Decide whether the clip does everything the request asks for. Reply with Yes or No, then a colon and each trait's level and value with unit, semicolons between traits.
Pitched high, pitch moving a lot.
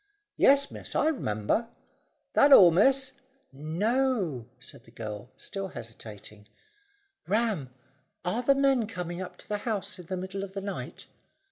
Yes: high, 195 Hz; wide, 9.0 semitones